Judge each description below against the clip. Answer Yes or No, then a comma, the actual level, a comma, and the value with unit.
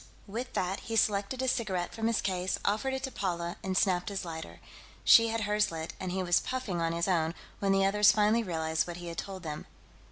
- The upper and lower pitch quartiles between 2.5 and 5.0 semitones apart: Yes, average, 3.6 semitones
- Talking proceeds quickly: Yes, fast, 225 wpm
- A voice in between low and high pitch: No, high, 195 Hz